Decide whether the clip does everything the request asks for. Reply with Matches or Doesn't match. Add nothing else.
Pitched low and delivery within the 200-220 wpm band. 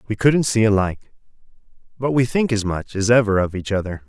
Matches